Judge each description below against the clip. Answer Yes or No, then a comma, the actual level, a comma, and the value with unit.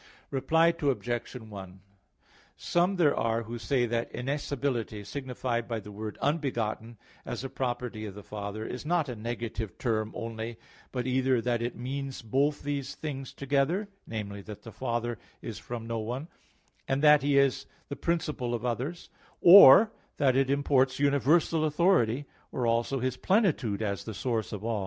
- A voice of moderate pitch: No, low, 125 Hz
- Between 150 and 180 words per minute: Yes, average, 160 wpm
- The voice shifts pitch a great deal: No, average, 3.8 semitones